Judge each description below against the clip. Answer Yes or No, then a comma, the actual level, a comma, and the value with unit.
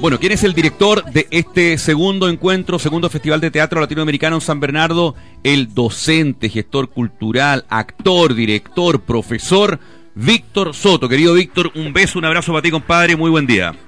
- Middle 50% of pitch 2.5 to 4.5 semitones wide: Yes, average, 3.9 semitones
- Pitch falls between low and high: Yes, medium, 160 Hz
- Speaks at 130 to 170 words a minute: Yes, average, 165 wpm